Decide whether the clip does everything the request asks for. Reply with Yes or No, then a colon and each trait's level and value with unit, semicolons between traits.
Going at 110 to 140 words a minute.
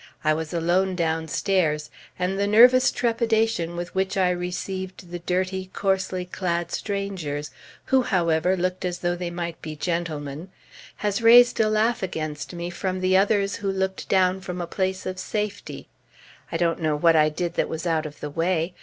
No: average, 175 wpm